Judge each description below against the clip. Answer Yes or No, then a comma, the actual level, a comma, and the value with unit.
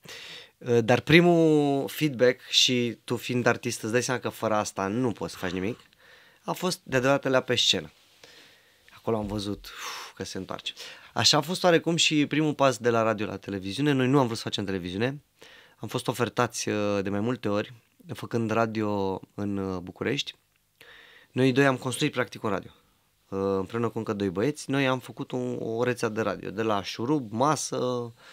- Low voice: Yes, low, 120 Hz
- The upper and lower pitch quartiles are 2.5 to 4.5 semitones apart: Yes, average, 4.0 semitones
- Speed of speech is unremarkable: No, fast, 175 wpm